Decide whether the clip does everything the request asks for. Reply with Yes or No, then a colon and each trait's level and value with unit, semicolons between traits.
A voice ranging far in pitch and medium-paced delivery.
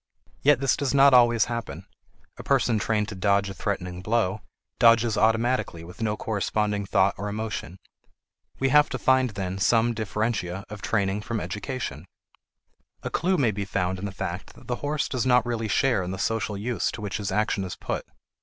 No: average, 3.5 semitones; average, 190 wpm